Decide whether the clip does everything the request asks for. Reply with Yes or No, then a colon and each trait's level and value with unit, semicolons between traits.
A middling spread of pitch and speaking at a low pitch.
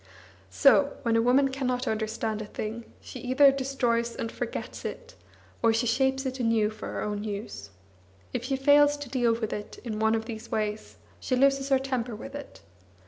No: average, 3.5 semitones; high, 240 Hz